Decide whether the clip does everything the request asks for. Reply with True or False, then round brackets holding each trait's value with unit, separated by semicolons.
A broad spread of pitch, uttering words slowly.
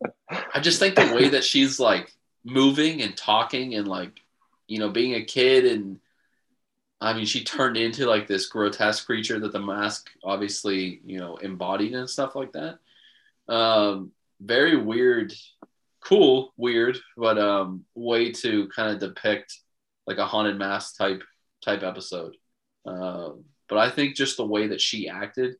False (5.7 semitones; 160 wpm)